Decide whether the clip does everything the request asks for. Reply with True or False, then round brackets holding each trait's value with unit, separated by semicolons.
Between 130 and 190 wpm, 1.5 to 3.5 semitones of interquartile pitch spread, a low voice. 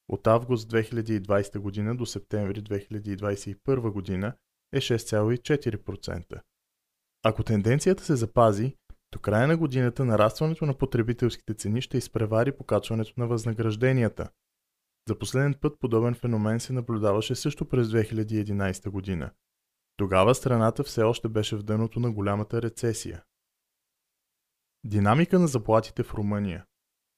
False (115 wpm; 3.0 semitones; 110 Hz)